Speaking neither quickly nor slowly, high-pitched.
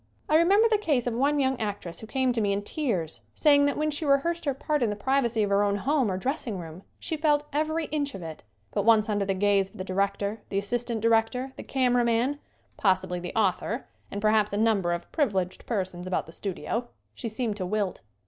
No: fast, 220 wpm; high, 225 Hz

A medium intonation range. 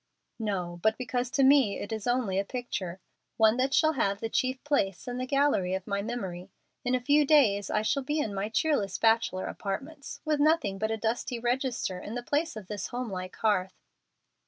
Yes: average, 5.0 semitones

